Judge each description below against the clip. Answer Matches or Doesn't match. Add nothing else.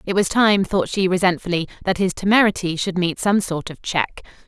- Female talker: Matches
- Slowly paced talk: Doesn't match